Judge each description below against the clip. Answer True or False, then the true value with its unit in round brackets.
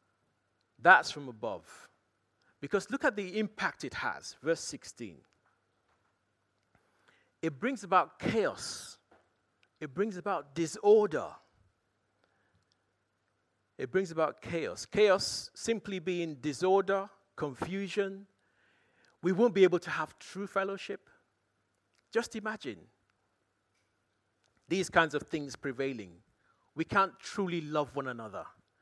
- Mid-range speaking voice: True (160 Hz)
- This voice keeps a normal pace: False (105 wpm)